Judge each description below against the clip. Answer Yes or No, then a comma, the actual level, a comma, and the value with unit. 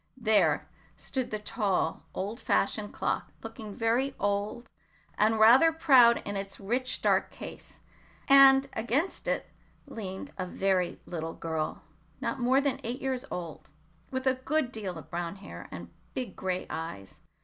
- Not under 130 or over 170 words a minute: Yes, average, 150 wpm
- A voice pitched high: Yes, high, 220 Hz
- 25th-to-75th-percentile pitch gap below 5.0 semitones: No, average, 5.3 semitones